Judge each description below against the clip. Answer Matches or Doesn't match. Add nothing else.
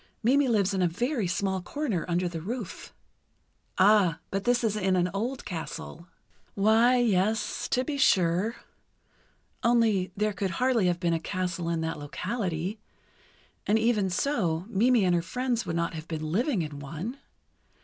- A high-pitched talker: Matches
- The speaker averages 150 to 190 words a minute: Matches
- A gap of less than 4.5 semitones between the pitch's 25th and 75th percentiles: Doesn't match